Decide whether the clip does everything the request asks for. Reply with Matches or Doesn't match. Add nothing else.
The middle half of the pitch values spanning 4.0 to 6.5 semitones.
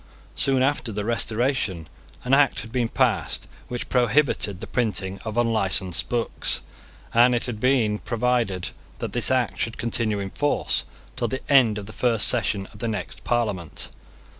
Doesn't match